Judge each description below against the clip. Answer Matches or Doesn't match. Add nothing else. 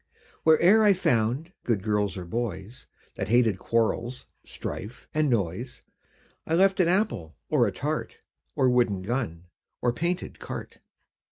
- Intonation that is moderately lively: Doesn't match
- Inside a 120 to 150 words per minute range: Matches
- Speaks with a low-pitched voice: Matches